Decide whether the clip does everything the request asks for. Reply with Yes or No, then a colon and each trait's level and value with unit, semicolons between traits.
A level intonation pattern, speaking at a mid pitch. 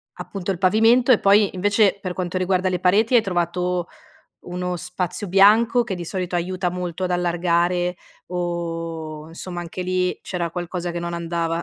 Yes: narrow, 1.7 semitones; medium, 180 Hz